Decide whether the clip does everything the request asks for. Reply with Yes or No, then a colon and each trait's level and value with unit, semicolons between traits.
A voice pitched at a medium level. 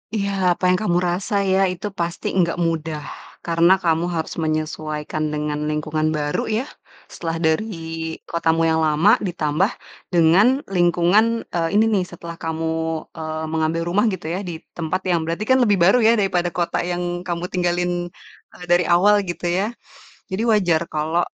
Yes: medium, 175 Hz